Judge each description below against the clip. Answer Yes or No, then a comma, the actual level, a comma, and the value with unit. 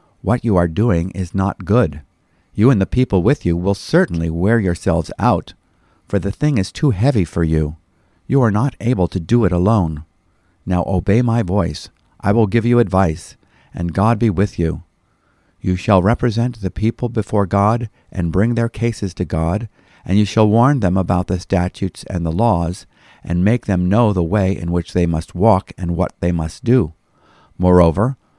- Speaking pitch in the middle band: No, very low, 95 Hz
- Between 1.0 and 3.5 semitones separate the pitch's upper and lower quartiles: No, average, 4.6 semitones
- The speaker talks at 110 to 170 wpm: No, average, 190 wpm